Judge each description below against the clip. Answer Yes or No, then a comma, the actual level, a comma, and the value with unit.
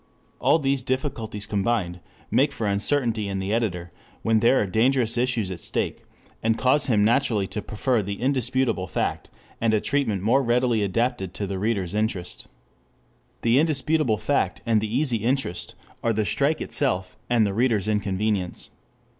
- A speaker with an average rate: Yes, average, 160 wpm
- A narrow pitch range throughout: No, average, 4.0 semitones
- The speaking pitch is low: Yes, low, 110 Hz